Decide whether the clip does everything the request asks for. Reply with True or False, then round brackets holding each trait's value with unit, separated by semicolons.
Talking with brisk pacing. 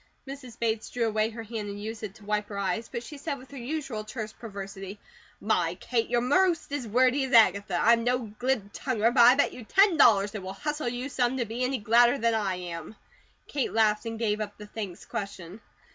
True (220 wpm)